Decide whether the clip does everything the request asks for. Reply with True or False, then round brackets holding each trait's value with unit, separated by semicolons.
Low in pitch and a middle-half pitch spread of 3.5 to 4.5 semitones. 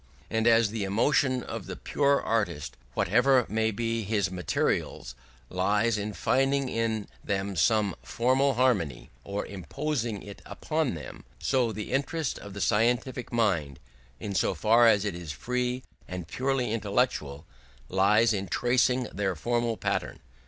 True (110 Hz; 4.1 semitones)